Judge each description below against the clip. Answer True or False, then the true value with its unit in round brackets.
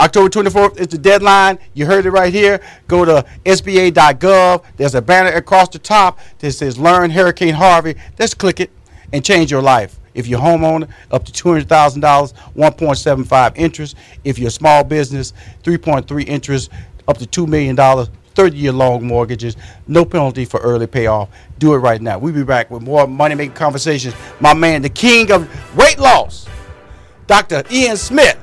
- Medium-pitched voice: True (150 Hz)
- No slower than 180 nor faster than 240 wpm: False (170 wpm)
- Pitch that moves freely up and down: True (5.9 semitones)